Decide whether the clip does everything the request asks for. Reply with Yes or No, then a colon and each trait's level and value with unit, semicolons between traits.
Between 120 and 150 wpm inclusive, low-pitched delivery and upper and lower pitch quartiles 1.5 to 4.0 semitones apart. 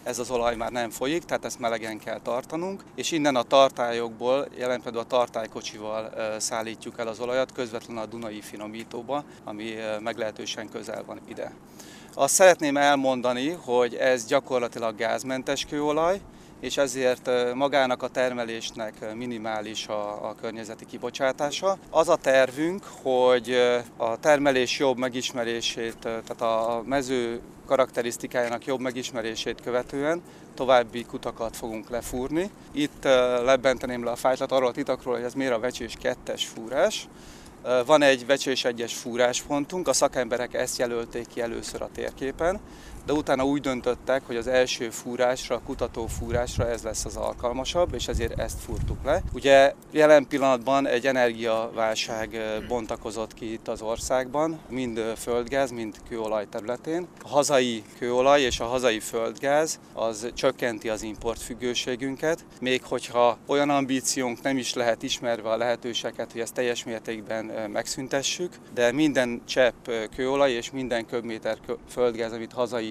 Yes: average, 140 wpm; low, 125 Hz; narrow, 2.6 semitones